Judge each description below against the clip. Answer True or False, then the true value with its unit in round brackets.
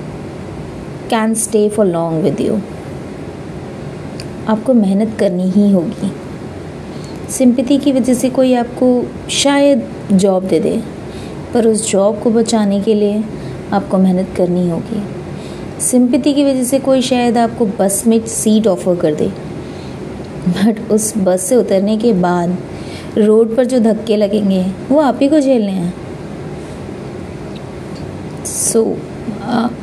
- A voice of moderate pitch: False (215 Hz)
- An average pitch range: True (4.1 semitones)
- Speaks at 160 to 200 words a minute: False (135 wpm)